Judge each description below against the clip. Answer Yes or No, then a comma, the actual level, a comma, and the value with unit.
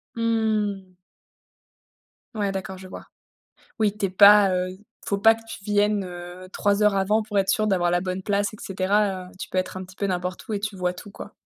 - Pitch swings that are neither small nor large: No, narrow, 2.1 semitones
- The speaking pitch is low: No, high, 195 Hz